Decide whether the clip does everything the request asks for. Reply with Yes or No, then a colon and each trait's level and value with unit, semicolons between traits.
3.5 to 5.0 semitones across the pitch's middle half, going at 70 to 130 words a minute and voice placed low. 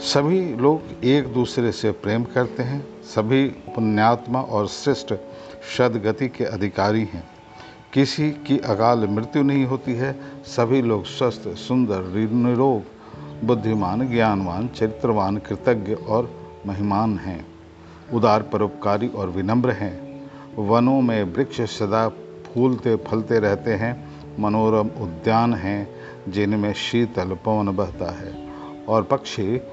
Yes: average, 4.0 semitones; average, 115 wpm; low, 110 Hz